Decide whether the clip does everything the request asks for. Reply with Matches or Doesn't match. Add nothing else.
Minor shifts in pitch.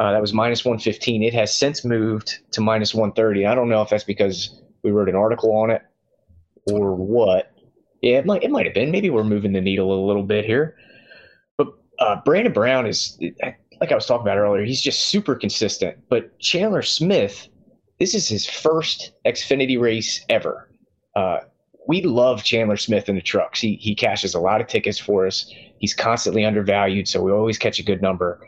Matches